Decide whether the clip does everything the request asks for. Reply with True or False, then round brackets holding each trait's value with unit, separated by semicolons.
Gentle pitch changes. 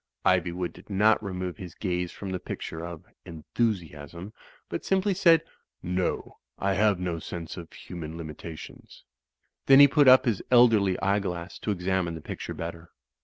False (3.7 semitones)